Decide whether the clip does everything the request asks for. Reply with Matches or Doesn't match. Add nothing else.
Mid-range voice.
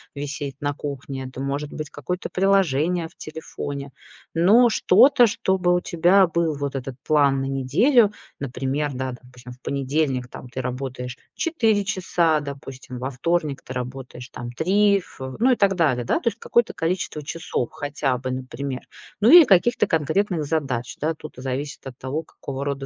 Matches